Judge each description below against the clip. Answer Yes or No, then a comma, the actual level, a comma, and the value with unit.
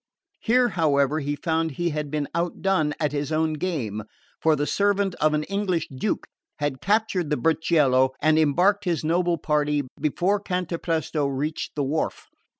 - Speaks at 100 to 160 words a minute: Yes, average, 155 wpm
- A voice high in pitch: No, medium, 155 Hz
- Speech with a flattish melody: No, average, 3.4 semitones